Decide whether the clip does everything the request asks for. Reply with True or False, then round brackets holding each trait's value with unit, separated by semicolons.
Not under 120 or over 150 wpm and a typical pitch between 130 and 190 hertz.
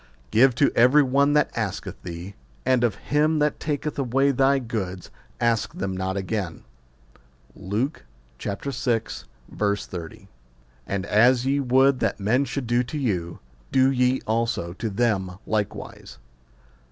False (135 wpm; 120 Hz)